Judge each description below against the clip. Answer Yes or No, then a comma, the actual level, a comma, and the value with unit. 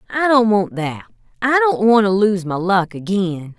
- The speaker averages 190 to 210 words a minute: Yes, average, 200 wpm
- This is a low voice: No, high, 205 Hz